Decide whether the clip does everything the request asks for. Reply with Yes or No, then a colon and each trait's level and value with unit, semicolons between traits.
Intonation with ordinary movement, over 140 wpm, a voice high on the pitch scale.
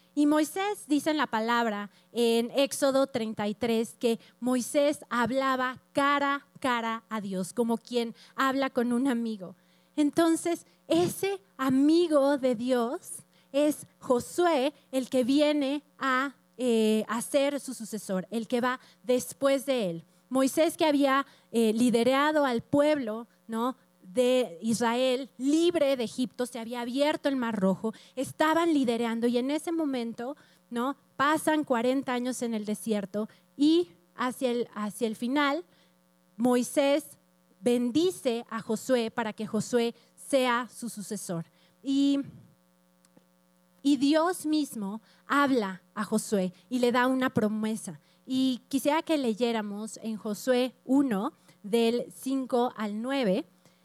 No: average, 4.1 semitones; average, 130 wpm; high, 245 Hz